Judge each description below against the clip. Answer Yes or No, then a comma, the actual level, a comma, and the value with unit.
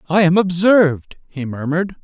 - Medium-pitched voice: Yes, medium, 170 Hz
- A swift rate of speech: No, average, 150 wpm